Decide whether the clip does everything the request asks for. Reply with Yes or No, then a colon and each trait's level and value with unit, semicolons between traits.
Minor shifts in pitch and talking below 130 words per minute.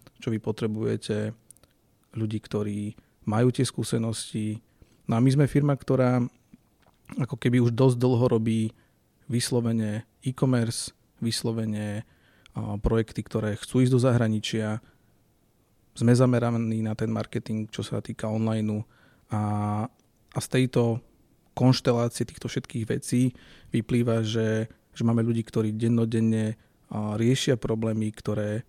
Yes: narrow, 2.3 semitones; average, 115 wpm